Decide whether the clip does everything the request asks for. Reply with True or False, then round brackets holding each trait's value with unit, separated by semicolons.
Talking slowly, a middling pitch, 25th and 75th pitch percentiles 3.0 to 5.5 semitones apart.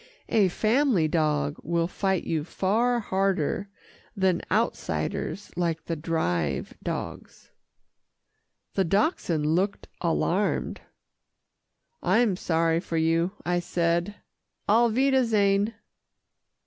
True (95 wpm; 180 Hz; 4.0 semitones)